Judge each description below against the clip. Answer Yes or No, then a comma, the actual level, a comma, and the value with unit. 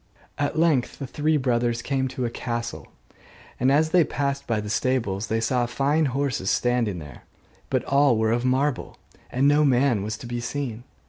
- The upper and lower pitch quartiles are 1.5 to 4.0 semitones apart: Yes, average, 3.1 semitones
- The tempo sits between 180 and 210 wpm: Yes, average, 185 wpm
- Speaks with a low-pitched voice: Yes, low, 125 Hz